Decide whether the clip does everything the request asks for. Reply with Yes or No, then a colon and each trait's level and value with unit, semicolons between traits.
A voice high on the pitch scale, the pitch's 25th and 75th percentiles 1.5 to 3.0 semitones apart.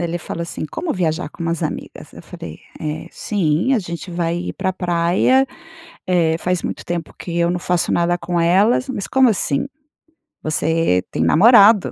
No: medium, 175 Hz; narrow, 2.5 semitones